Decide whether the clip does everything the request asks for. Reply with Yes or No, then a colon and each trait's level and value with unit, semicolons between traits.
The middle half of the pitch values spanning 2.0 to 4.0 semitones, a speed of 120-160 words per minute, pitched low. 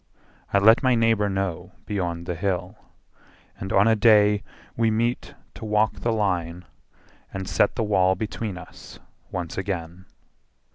Yes: average, 3.2 semitones; average, 145 wpm; low, 100 Hz